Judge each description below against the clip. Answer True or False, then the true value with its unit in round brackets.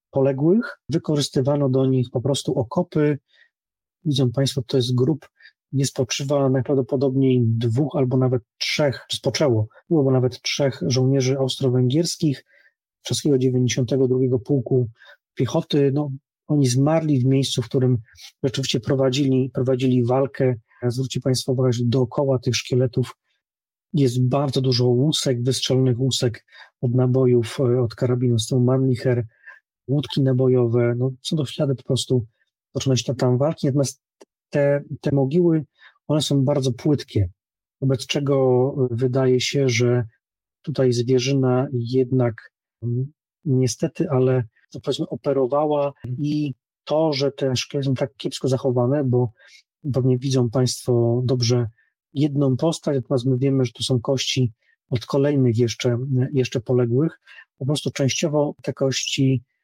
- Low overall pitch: True (130 Hz)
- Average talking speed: True (130 wpm)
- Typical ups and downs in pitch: False (1.9 semitones)